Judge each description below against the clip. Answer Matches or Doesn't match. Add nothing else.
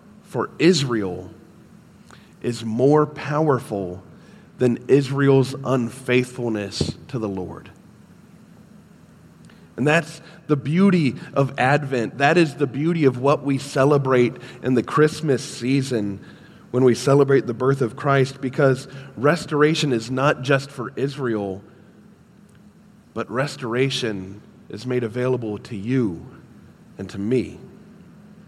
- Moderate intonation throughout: Matches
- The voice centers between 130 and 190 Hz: Matches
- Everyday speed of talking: Doesn't match